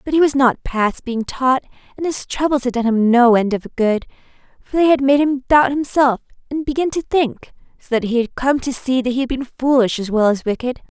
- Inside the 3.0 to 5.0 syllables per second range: No, 5.3 syllables/s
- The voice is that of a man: No, female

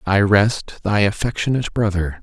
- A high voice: No, low, 100 Hz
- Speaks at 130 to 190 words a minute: Yes, slow, 135 wpm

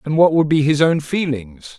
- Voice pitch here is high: No, medium, 145 Hz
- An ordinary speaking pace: No, fast, 235 wpm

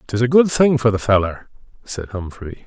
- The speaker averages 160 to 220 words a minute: Yes, fast, 205 wpm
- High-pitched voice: No, low, 115 Hz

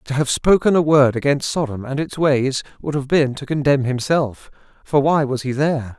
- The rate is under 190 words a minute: No, average, 200 wpm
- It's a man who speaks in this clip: Yes, male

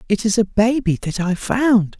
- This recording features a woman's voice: No, male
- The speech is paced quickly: Yes, fast, 210 wpm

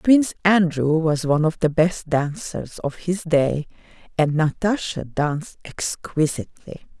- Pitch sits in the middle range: Yes, medium, 160 Hz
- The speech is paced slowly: Yes, slow, 130 wpm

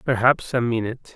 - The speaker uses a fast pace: No, average, 155 wpm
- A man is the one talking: Yes, male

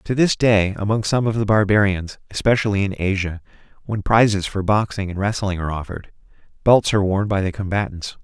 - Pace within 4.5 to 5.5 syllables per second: No, 5.8 syllables/s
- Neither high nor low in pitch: No, low, 100 Hz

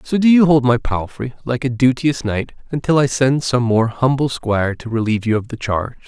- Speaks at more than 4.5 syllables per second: Yes, 5.5 syllables/s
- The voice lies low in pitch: Yes, low, 125 Hz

